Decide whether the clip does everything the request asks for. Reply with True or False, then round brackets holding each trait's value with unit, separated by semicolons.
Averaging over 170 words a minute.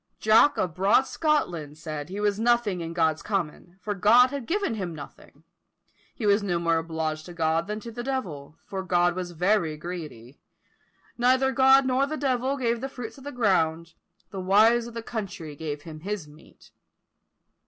True (180 wpm)